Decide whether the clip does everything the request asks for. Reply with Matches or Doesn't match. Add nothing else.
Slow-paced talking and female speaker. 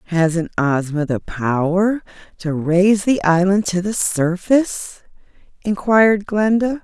Matches